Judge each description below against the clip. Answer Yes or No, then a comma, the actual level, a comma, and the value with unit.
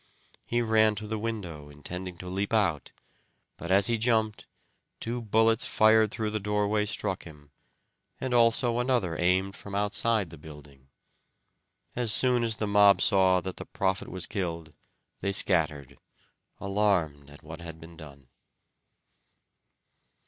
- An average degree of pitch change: Yes, average, 4.8 semitones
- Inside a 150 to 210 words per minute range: No, average, 140 wpm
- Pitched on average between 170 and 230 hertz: No, low, 100 Hz